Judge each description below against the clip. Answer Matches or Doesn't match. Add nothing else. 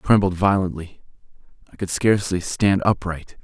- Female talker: Doesn't match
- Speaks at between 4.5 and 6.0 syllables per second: Matches